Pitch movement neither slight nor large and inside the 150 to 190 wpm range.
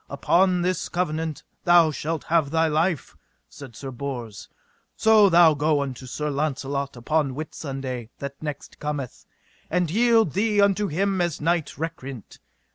No: average, 4.0 semitones; average, 140 wpm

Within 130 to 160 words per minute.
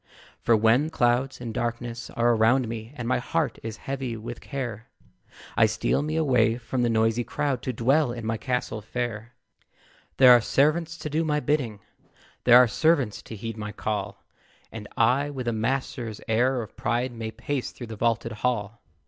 No: average, 180 wpm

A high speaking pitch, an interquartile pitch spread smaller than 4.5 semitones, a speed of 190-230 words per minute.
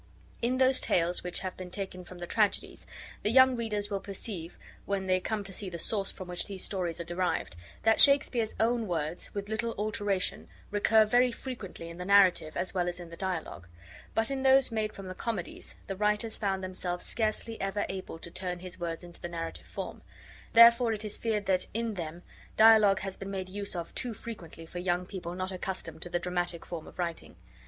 Yes: high, 195 Hz; average, 3.6 semitones; fast, 205 wpm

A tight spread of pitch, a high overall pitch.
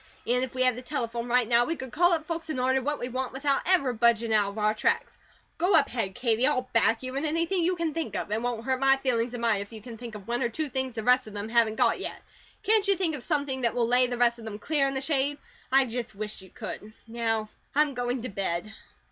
No: average, 3.3 semitones; very high, 250 Hz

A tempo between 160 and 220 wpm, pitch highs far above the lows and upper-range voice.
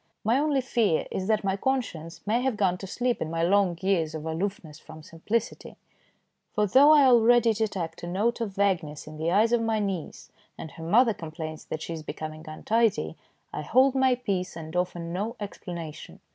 Yes: average, 190 wpm; wide, 5.9 semitones; high, 195 Hz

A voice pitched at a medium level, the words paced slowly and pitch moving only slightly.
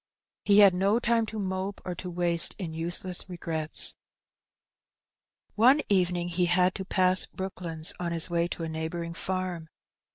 No: medium, 180 Hz; average, 155 wpm; narrow, 2.1 semitones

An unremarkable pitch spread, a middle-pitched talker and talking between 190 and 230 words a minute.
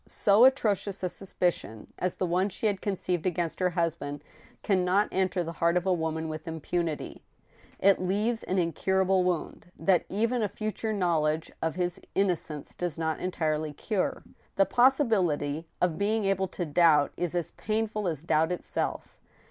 No: average, 3.5 semitones; medium, 180 Hz; average, 165 wpm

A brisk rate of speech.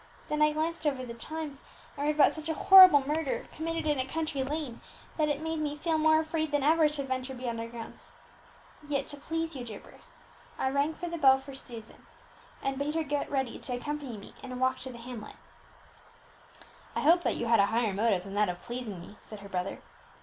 Yes: fast, 220 wpm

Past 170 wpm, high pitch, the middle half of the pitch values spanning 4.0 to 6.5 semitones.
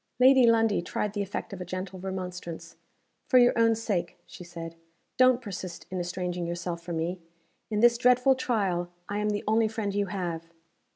Yes: average, 180 wpm; high, 195 Hz; average, 4.3 semitones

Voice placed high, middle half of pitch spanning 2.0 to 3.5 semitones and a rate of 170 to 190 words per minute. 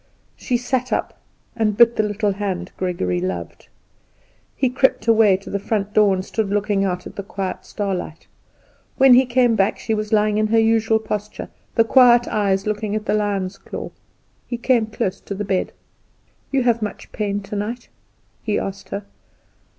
Yes: high, 210 Hz; narrow, 2.4 semitones; average, 175 wpm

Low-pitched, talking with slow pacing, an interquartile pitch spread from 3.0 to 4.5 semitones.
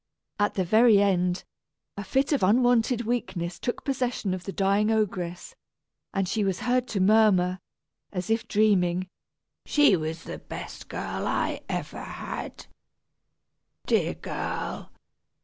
No: high, 200 Hz; slow, 130 wpm; average, 3.9 semitones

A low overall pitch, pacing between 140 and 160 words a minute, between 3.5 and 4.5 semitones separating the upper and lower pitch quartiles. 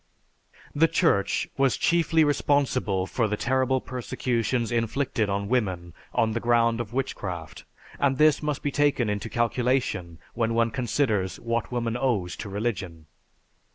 Yes: low, 120 Hz; average, 145 wpm; average, 4.2 semitones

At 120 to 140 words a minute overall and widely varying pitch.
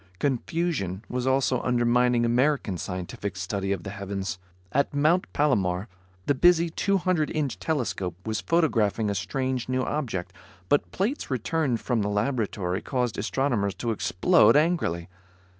Yes: slow, 135 wpm; wide, 6.5 semitones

